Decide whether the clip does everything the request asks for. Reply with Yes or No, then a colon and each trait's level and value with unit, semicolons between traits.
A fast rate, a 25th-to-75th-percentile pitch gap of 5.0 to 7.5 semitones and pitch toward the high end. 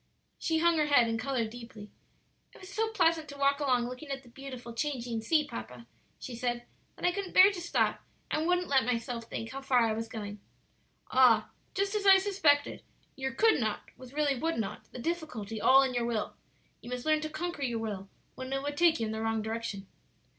Yes: fast, 215 wpm; average, 5.3 semitones; very high, 260 Hz